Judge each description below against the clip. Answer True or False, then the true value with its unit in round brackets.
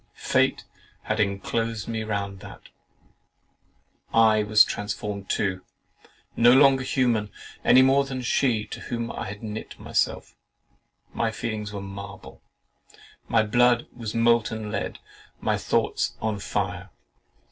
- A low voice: True (110 Hz)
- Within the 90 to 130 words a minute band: True (125 wpm)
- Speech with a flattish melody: True (2.2 semitones)